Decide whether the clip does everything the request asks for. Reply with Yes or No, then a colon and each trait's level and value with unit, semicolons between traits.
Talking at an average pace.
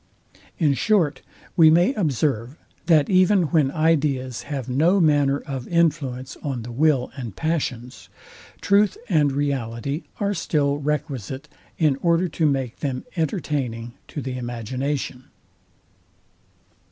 No: slow, 120 wpm